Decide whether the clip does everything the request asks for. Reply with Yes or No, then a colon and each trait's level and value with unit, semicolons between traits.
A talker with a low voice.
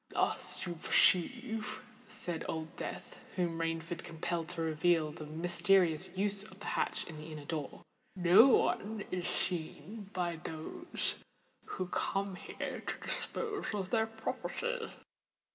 No: medium, 175 Hz